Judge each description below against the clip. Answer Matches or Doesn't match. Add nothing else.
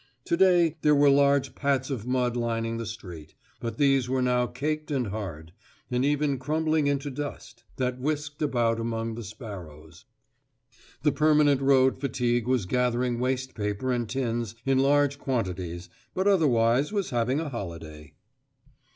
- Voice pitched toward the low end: Matches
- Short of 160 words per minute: Matches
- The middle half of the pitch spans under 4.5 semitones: Matches